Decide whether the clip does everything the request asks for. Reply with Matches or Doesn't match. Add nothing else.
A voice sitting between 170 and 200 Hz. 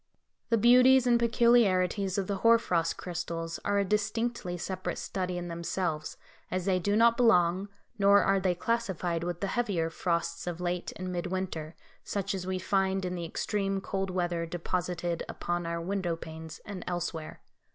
Matches